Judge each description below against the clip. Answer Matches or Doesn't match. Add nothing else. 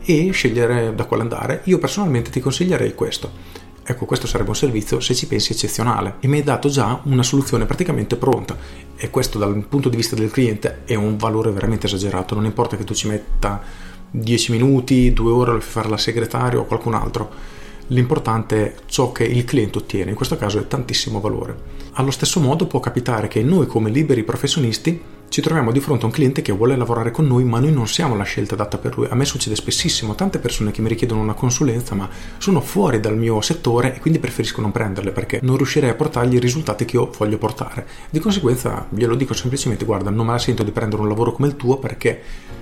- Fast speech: Matches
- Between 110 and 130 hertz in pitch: Matches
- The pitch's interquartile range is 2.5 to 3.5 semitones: Doesn't match